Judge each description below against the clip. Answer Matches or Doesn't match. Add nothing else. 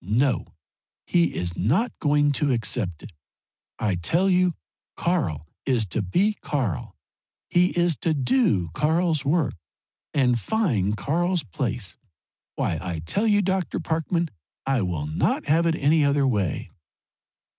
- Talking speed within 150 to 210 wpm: Doesn't match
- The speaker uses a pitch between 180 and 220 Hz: Doesn't match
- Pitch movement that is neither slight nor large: Doesn't match